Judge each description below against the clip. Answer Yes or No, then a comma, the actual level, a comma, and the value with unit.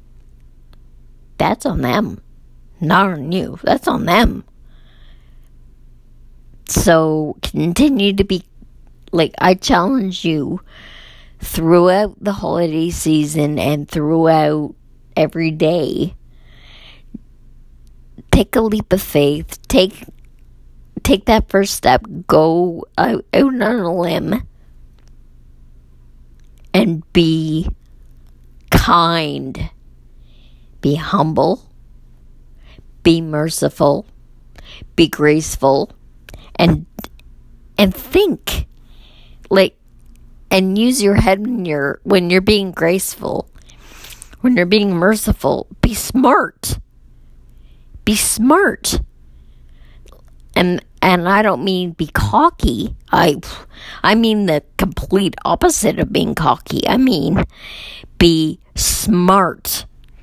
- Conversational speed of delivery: No, slow, 90 wpm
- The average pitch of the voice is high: No, medium, 160 Hz